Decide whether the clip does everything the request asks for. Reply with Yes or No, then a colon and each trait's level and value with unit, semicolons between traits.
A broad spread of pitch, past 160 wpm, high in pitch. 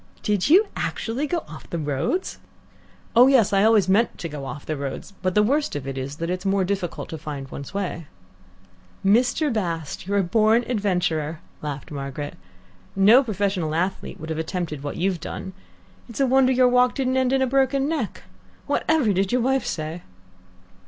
Yes: wide, 7.7 semitones; average, 185 wpm; high, 195 Hz